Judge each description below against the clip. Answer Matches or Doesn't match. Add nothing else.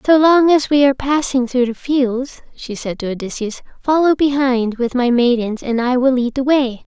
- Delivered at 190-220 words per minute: Matches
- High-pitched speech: Matches